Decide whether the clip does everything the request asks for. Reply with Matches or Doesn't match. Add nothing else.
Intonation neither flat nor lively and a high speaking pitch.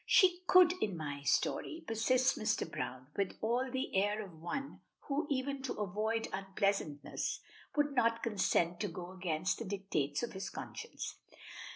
Doesn't match